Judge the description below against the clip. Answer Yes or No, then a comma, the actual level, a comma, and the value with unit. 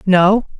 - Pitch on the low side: No, high, 195 Hz